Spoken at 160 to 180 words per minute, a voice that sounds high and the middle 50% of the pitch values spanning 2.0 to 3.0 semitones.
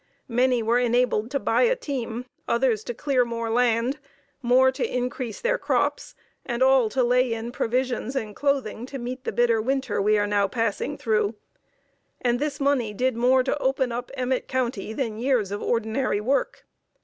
Yes: average, 175 wpm; high, 245 Hz; narrow, 2.5 semitones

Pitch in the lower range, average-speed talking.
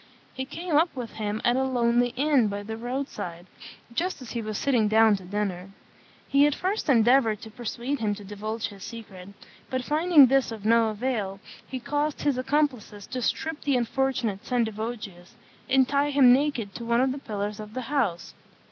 No: high, 235 Hz; average, 190 wpm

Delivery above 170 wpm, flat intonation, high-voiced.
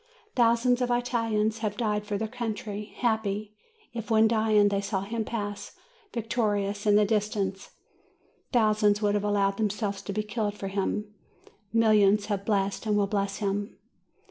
No: average, 160 wpm; narrow, 1.6 semitones; high, 210 Hz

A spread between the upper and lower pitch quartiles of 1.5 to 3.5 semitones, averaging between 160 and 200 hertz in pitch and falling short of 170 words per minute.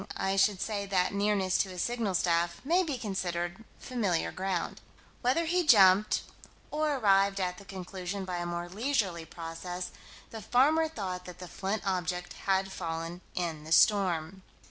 Yes: average, 3.1 semitones; high, 190 Hz; average, 160 wpm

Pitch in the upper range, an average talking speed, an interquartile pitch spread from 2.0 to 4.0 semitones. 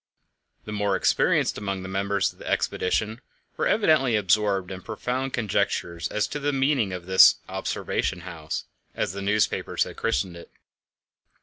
No: low, 100 Hz; average, 150 wpm; average, 3.4 semitones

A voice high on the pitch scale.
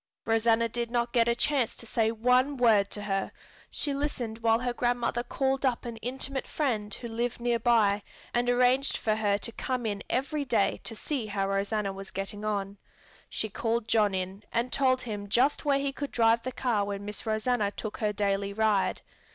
Yes: high, 230 Hz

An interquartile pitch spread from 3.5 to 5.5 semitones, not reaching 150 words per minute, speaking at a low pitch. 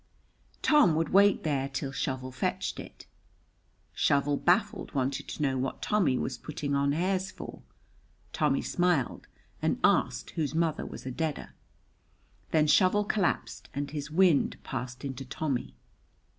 No: average, 4.7 semitones; average, 140 wpm; medium, 145 Hz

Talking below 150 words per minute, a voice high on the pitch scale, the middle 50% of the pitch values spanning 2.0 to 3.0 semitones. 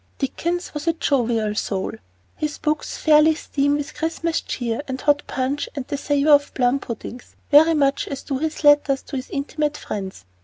No: average, 180 wpm; very high, 285 Hz; narrow, 2.6 semitones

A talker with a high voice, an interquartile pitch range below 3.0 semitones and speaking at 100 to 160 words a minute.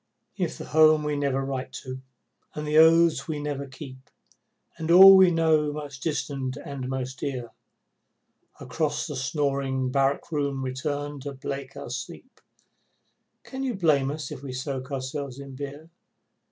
No: medium, 140 Hz; narrow, 2.6 semitones; average, 155 wpm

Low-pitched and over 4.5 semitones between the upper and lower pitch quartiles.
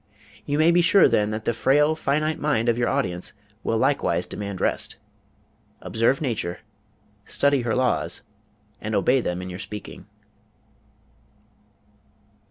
Yes: low, 120 Hz; wide, 5.5 semitones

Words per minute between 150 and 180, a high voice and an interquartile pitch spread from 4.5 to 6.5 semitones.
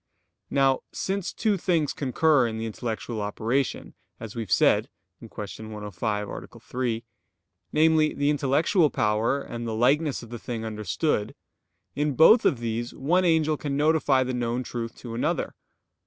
No: average, 155 wpm; low, 125 Hz; average, 5.0 semitones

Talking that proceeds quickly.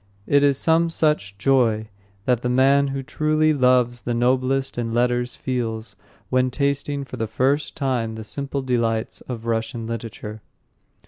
No: average, 150 wpm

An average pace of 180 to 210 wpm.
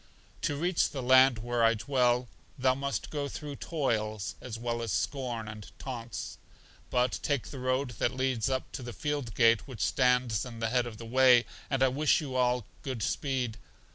Yes: average, 190 wpm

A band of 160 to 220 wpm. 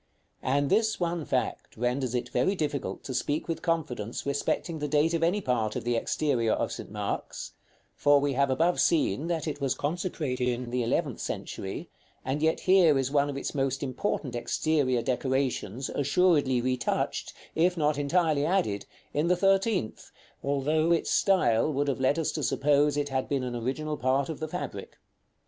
Yes: average, 175 wpm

